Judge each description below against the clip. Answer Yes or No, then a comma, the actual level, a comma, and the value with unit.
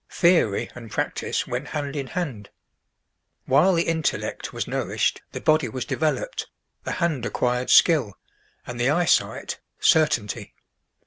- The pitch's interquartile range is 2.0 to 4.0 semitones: No, average, 5.1 semitones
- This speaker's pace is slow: Yes, slow, 130 wpm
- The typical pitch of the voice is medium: Yes, medium, 145 Hz